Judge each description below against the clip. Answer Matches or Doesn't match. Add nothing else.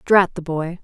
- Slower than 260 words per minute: Matches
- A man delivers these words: Doesn't match